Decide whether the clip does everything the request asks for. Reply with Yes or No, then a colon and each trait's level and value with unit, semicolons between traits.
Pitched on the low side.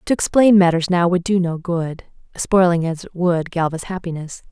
No: medium, 175 Hz